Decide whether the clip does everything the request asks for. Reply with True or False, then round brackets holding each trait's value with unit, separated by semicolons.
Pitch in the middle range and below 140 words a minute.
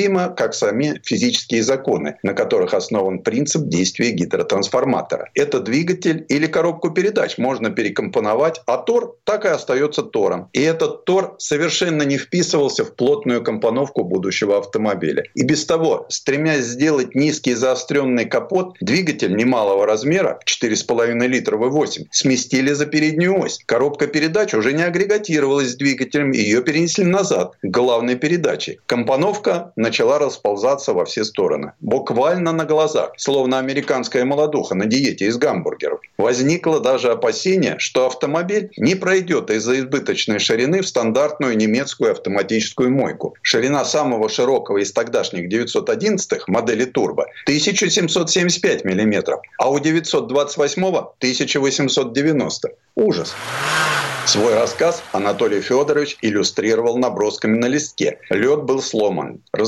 True (165 Hz; 125 wpm)